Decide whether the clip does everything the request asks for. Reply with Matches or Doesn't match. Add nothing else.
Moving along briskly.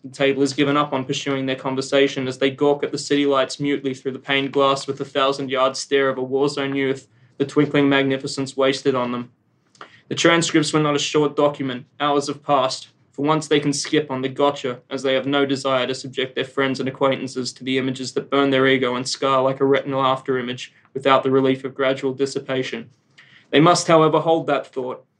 Matches